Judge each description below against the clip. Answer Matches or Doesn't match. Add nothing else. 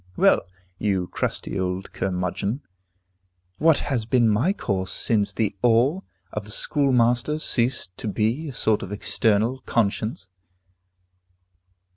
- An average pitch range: Matches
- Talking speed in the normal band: Doesn't match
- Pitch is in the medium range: Doesn't match